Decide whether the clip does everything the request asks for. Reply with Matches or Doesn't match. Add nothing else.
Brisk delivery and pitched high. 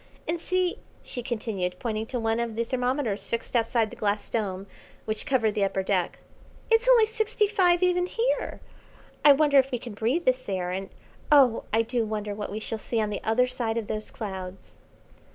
Doesn't match